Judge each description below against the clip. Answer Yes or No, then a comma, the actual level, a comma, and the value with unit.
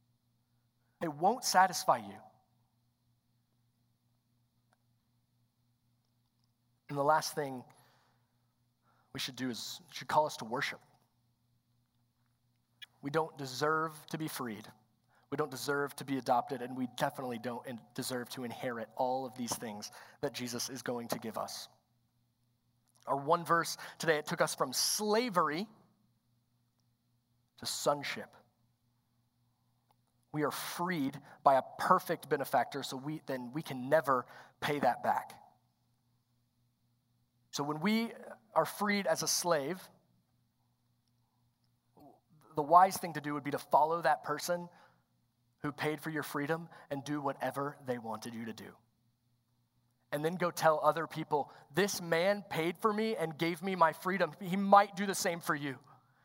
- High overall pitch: No, low, 130 Hz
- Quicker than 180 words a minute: No, average, 140 wpm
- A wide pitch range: No, average, 4.7 semitones